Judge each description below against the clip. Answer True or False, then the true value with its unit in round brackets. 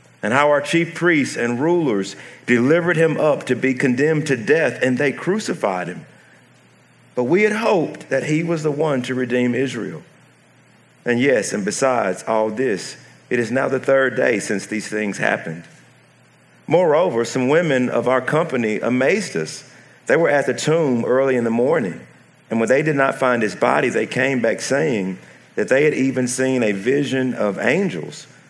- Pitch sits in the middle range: False (130 Hz)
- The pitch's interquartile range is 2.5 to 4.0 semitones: True (3.4 semitones)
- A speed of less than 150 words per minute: False (180 wpm)